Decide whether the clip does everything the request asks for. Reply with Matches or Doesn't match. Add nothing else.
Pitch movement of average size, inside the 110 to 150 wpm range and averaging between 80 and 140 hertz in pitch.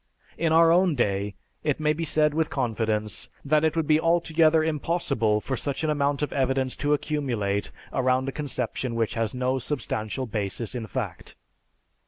Doesn't match